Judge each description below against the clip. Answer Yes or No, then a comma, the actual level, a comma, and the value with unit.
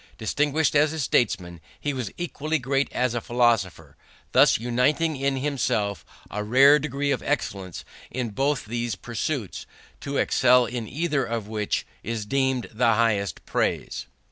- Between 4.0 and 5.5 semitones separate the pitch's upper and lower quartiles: Yes, average, 4.3 semitones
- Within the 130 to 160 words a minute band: Yes, average, 145 wpm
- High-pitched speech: No, low, 125 Hz